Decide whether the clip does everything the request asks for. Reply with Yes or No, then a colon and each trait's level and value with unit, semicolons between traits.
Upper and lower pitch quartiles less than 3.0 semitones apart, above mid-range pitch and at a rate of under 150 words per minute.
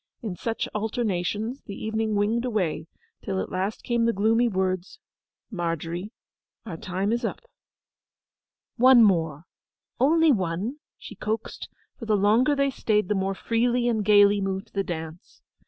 No: average, 3.6 semitones; high, 210 Hz; average, 140 wpm